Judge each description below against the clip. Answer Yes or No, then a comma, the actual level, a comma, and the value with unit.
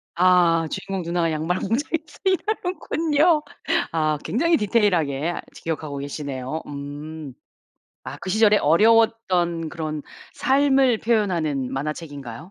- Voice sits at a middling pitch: Yes, medium, 170 Hz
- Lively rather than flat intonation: Yes, wide, 7.0 semitones